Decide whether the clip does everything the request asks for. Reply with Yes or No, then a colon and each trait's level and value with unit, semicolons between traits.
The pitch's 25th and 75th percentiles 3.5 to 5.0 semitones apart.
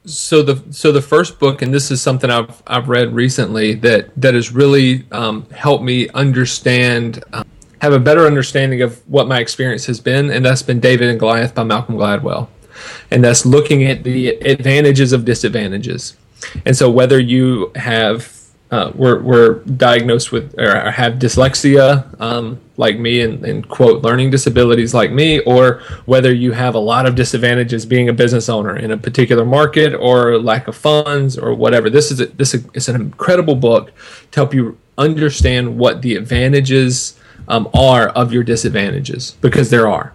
No: narrow, 2.6 semitones